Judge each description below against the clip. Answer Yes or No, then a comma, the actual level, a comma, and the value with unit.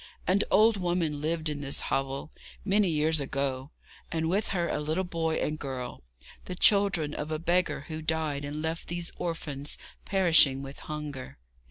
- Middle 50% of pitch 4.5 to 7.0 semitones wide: No, average, 3.3 semitones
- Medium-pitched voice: Yes, medium, 160 Hz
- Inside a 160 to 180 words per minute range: Yes, average, 165 wpm